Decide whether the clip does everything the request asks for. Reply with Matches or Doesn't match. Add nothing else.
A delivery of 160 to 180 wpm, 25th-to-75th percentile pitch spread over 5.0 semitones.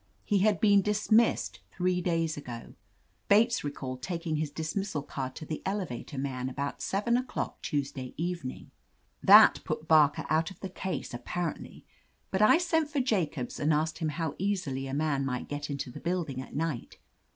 Matches